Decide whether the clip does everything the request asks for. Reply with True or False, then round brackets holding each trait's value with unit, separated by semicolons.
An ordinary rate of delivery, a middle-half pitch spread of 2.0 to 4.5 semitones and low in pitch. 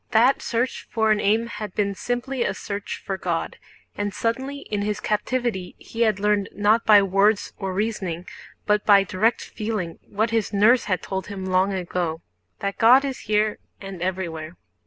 False (175 wpm; 2.9 semitones; 210 Hz)